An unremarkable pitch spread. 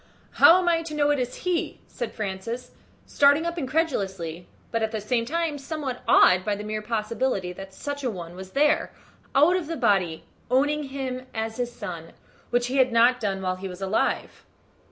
No: wide, 6.8 semitones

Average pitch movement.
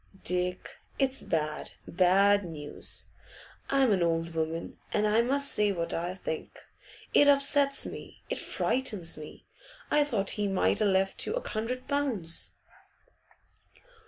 No: wide, 7.5 semitones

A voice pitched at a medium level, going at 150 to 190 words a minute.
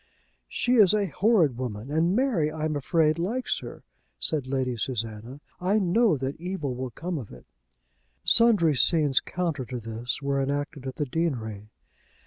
Yes: medium, 150 Hz; average, 160 wpm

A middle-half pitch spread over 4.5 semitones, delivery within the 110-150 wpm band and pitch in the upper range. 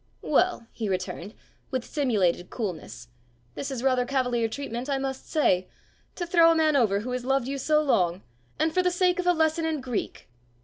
No: wide, 5.5 semitones; average, 190 wpm; very high, 265 Hz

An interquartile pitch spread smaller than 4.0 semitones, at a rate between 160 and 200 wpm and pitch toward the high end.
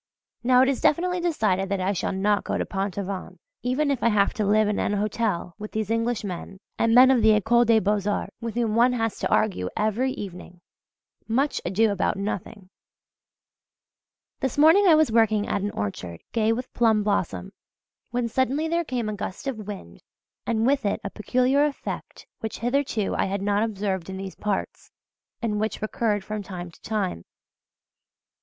Yes: average, 3.5 semitones; average, 180 wpm; high, 215 Hz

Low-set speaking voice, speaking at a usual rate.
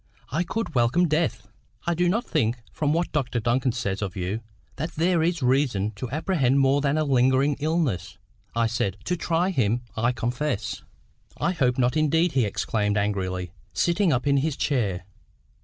Yes: low, 130 Hz; average, 170 wpm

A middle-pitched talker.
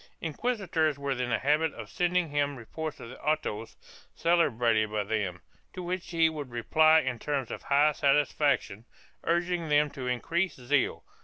Yes: medium, 145 Hz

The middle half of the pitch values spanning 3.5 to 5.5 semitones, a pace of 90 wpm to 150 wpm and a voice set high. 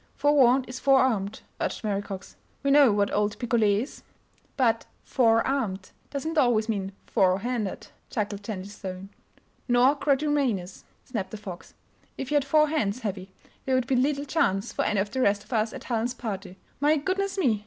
No: average, 5.1 semitones; average, 175 wpm; high, 230 Hz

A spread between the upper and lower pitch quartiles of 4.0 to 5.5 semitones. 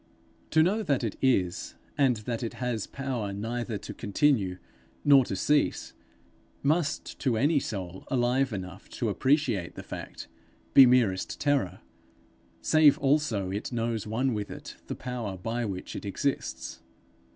Yes: average, 5.2 semitones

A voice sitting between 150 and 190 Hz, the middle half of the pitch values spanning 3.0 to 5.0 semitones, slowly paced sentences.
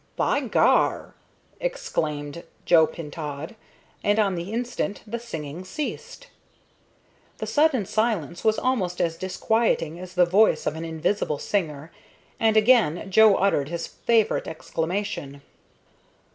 No: medium, 185 Hz; wide, 5.4 semitones; slow, 120 wpm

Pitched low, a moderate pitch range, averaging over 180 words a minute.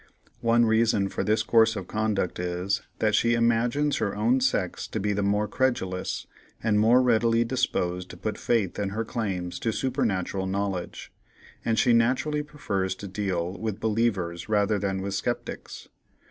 No: low, 105 Hz; average, 3.3 semitones; average, 160 wpm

